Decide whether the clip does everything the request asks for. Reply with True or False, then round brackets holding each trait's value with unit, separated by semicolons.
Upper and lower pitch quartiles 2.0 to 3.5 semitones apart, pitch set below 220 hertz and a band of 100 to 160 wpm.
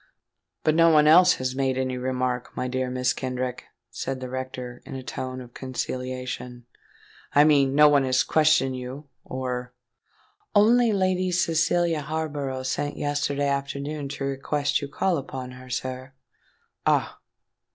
True (2.8 semitones; 135 Hz; 140 wpm)